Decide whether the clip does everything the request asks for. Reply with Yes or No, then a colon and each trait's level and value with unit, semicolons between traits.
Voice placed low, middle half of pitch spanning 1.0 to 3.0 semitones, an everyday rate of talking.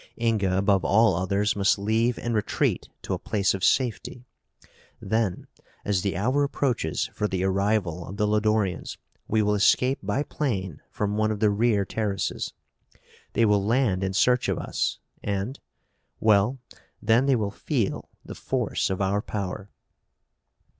Yes: low, 105 Hz; narrow, 2.6 semitones; average, 155 wpm